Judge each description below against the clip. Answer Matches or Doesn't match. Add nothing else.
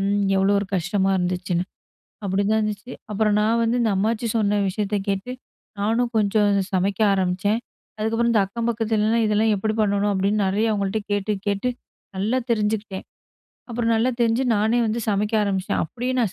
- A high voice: Matches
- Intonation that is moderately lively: Doesn't match